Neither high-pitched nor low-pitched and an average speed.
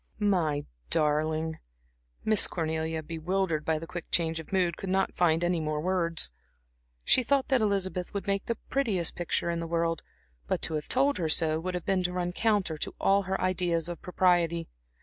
Yes: medium, 175 Hz; average, 180 wpm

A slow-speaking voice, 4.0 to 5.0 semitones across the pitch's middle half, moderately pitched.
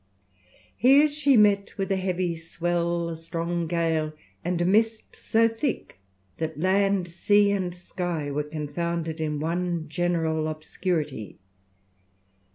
No: slow, 125 wpm; average, 3.4 semitones; medium, 175 Hz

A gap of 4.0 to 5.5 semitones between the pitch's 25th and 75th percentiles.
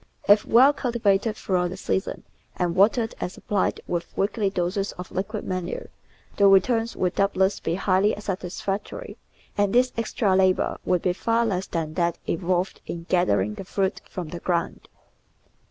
No: average, 2.7 semitones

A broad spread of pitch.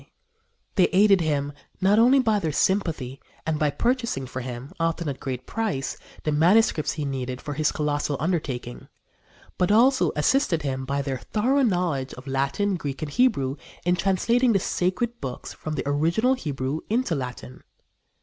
Yes: wide, 6.8 semitones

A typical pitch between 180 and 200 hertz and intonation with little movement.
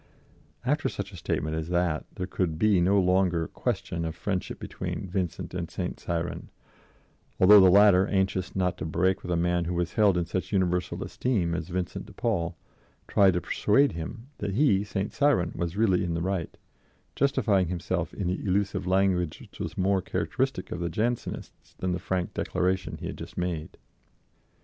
No: very low, 90 Hz; narrow, 2.3 semitones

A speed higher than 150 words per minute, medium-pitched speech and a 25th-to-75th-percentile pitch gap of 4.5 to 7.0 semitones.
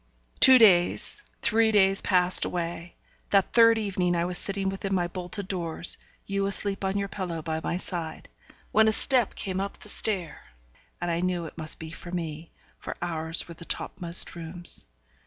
No: average, 180 wpm; medium, 180 Hz; average, 2.7 semitones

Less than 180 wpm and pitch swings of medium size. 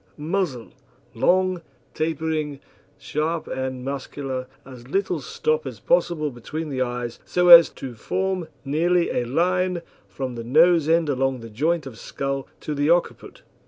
Yes: average, 145 wpm; average, 4.7 semitones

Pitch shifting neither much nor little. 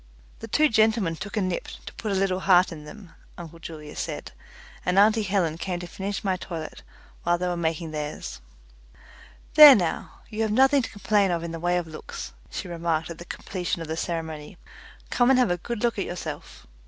Yes: average, 4.0 semitones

